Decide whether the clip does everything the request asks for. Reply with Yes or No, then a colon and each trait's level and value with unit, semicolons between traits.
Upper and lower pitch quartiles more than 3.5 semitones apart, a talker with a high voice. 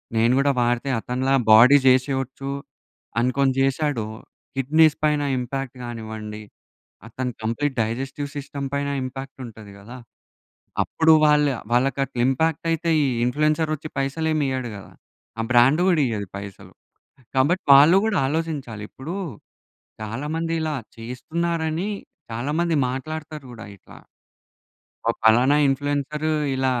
No: average, 3.9 semitones; low, 135 Hz